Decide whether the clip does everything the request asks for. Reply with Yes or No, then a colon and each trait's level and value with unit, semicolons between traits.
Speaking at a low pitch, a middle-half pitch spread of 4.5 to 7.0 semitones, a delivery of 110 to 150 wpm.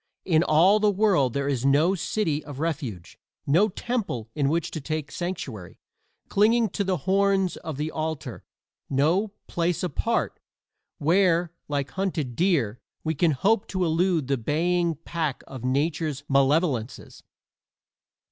No: medium, 160 Hz; average, 4.8 semitones; average, 140 wpm